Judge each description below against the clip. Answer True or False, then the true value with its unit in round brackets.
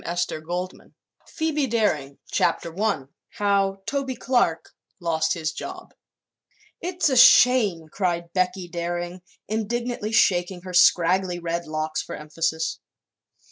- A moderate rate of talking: False (115 wpm)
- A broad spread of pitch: False (4.5 semitones)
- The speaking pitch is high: False (180 Hz)